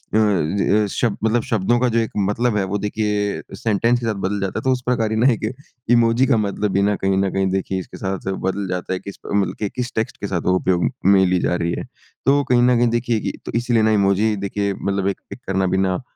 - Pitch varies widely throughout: No, average, 3.1 semitones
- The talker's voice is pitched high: No, low, 105 Hz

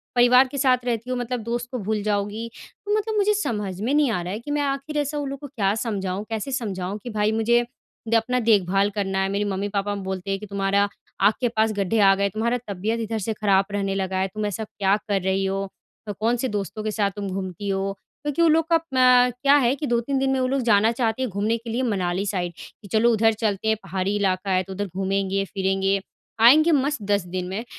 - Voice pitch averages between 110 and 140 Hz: No, high, 215 Hz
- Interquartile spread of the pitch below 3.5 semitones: No, average, 3.8 semitones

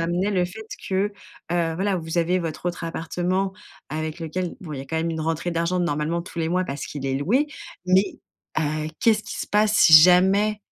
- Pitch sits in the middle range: Yes, medium, 175 Hz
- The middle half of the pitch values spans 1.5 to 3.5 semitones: Yes, average, 2.8 semitones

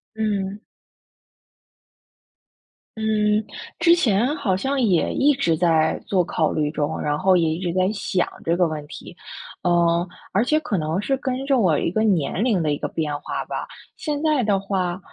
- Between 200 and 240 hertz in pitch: No, high, 190 Hz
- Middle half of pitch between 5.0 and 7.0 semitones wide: Yes, average, 5.3 semitones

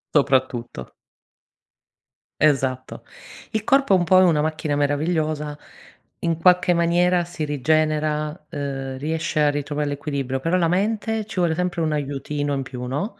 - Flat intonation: No, average, 3.4 semitones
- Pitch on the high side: No, medium, 155 Hz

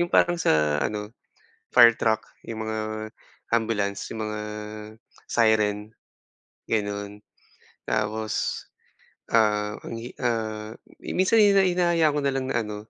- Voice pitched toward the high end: No, low, 110 Hz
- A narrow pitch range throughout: Yes, narrow, 2.3 semitones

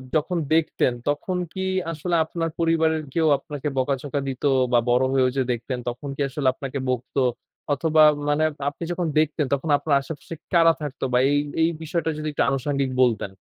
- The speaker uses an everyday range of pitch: Yes, average, 3.3 semitones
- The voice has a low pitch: No, medium, 145 Hz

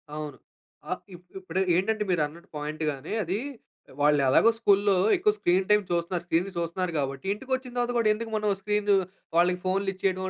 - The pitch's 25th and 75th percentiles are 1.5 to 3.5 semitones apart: No, average, 3.9 semitones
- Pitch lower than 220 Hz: Yes, medium, 185 Hz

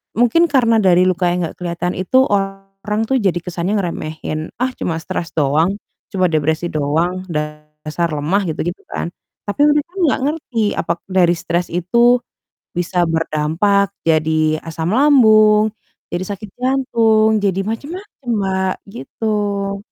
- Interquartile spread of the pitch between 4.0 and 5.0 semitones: Yes, average, 4.5 semitones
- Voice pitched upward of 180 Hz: Yes, high, 190 Hz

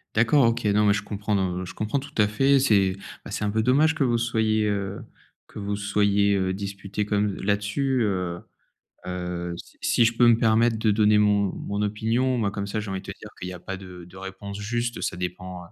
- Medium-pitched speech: No, low, 105 Hz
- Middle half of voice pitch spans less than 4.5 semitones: Yes, narrow, 2.6 semitones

